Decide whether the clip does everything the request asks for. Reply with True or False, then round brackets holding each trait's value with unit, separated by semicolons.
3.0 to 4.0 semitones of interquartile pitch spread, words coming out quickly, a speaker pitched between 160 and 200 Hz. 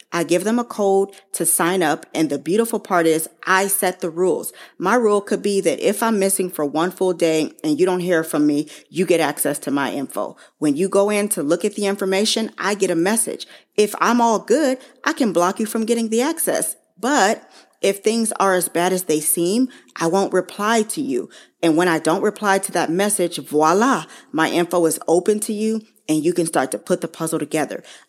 False (4.4 semitones; 225 wpm; 185 Hz)